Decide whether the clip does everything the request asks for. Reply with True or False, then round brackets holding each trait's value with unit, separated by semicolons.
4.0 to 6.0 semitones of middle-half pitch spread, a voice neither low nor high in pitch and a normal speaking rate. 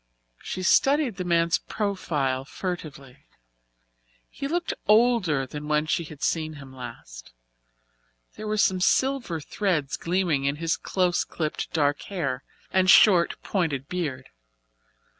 False (4.9 semitones; 165 Hz; 125 wpm)